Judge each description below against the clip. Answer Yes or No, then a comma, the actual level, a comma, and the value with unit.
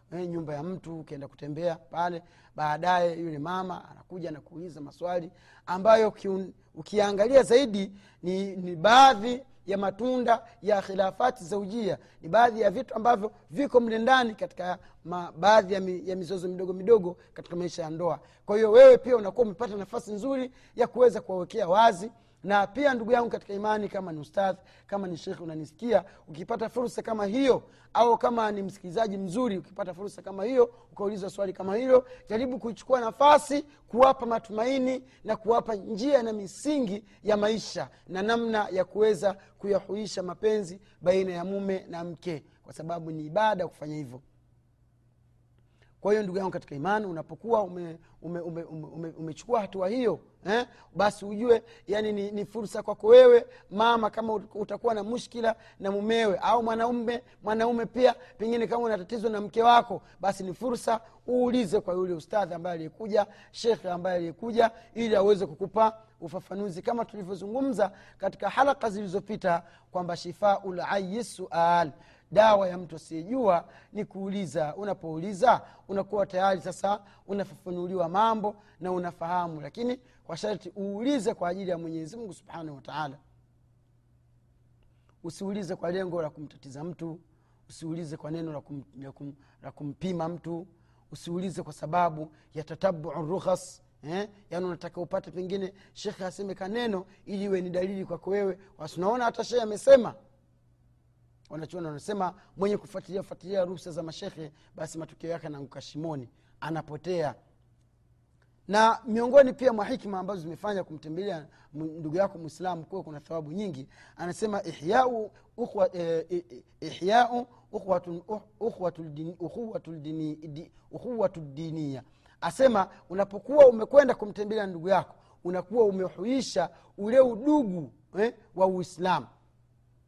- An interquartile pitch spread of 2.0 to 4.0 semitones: No, average, 4.8 semitones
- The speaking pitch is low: No, high, 190 Hz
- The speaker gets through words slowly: No, average, 130 wpm